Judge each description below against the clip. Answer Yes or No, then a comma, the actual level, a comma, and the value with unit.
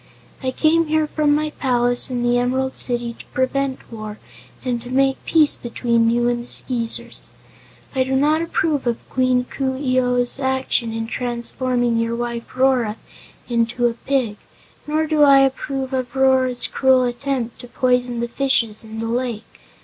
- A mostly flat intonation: Yes, narrow, 2.0 semitones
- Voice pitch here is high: Yes, very high, 250 Hz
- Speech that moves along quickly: No, average, 165 wpm